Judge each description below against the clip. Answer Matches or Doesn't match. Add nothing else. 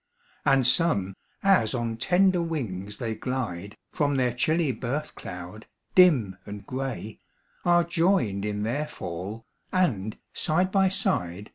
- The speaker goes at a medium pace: Doesn't match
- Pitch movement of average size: Doesn't match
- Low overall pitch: Matches